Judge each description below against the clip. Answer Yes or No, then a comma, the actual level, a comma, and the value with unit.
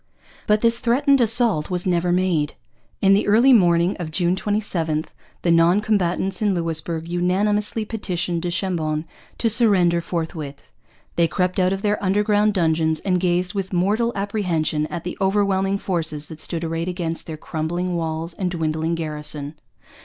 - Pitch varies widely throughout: No, average, 3.5 semitones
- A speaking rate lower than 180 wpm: Yes, average, 155 wpm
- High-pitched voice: No, medium, 180 Hz